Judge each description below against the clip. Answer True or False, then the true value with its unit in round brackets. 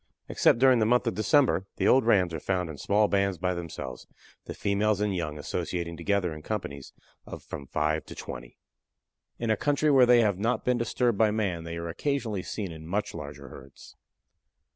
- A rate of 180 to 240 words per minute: True (195 wpm)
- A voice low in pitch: True (100 Hz)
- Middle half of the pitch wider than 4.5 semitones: True (5.3 semitones)